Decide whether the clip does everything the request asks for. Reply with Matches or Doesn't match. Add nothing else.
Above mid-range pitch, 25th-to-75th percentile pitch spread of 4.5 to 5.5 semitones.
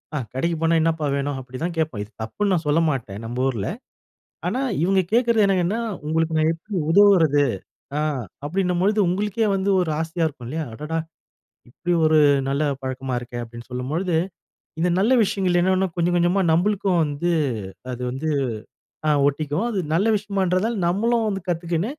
Doesn't match